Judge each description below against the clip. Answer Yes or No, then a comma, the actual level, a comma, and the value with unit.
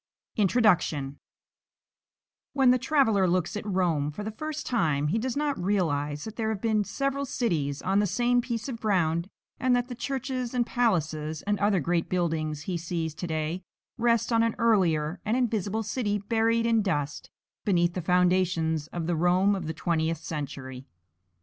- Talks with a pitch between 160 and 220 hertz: Yes, high, 190 Hz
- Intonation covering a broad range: Yes, wide, 6.1 semitones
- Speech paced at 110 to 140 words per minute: No, average, 170 wpm